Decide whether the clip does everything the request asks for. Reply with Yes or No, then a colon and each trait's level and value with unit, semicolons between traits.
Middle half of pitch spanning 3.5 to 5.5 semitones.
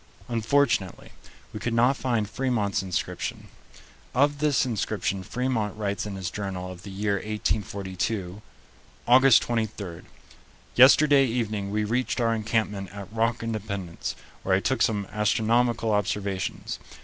No: average, 3.1 semitones